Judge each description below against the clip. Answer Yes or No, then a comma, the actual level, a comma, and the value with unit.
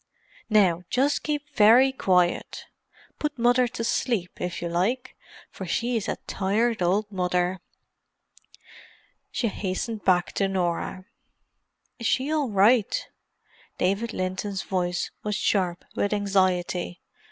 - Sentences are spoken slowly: Yes, slow, 115 wpm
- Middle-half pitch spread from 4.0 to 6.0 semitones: Yes, average, 4.4 semitones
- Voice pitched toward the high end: Yes, high, 200 Hz